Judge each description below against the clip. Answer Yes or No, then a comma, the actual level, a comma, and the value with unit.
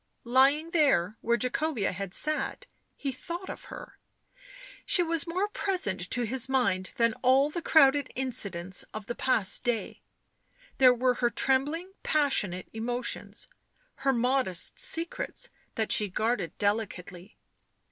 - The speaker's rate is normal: No, slow, 130 wpm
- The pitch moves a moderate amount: No, wide, 5.7 semitones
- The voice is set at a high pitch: Yes, very high, 250 Hz